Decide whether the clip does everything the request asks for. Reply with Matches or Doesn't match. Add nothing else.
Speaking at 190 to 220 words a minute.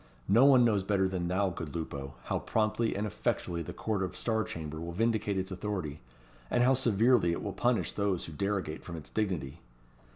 Matches